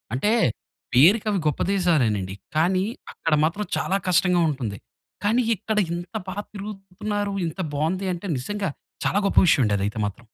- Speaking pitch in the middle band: Yes, medium, 180 Hz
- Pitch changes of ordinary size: No, wide, 6.0 semitones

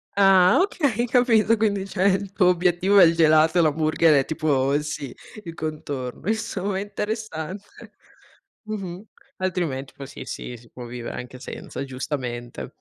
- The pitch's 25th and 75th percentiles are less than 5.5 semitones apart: No, wide, 5.9 semitones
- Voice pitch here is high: No, medium, 175 Hz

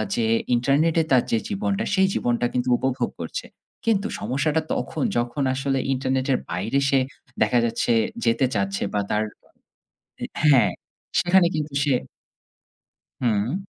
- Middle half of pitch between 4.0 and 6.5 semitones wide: Yes, average, 4.5 semitones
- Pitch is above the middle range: No, low, 130 Hz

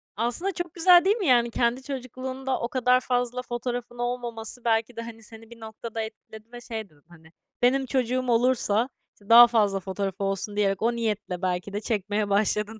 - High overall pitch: Yes, high, 235 Hz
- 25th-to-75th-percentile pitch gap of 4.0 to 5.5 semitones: No, average, 2.9 semitones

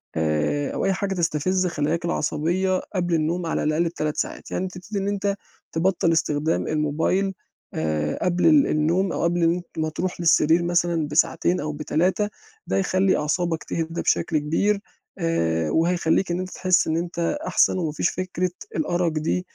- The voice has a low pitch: No, medium, 170 Hz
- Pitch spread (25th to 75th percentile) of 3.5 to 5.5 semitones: No, average, 3.0 semitones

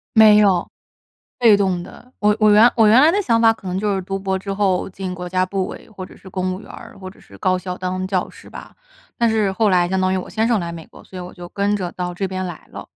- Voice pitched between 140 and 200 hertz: Yes, high, 190 Hz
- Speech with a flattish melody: Yes, narrow, 2.3 semitones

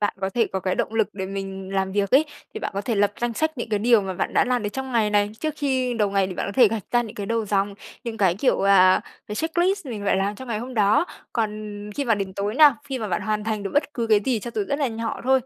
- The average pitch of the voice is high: Yes, high, 215 Hz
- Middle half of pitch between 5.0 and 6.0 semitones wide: No, average, 3.9 semitones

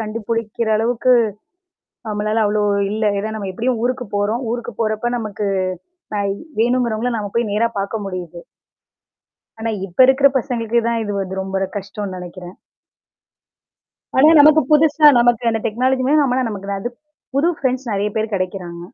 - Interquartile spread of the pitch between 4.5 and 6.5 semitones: No, average, 3.2 semitones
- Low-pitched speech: No, high, 220 Hz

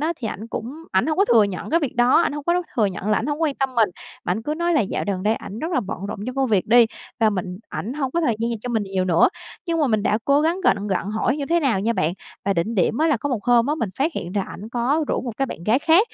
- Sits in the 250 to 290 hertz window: No, high, 240 Hz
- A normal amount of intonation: No, wide, 6.1 semitones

